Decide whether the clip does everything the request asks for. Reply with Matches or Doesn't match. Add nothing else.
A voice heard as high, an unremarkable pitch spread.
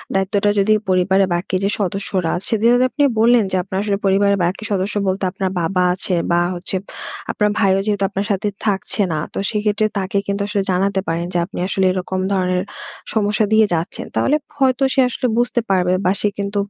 Doesn't match